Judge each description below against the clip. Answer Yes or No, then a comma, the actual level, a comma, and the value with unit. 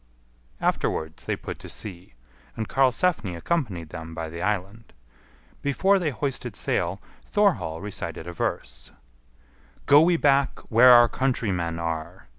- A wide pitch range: Yes, wide, 8.6 semitones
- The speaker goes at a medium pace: No, slow, 130 wpm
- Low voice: Yes, low, 105 Hz